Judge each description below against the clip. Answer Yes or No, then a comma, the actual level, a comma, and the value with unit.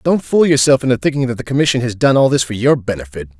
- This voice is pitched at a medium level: No, low, 125 Hz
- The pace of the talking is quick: Yes, fast, 265 wpm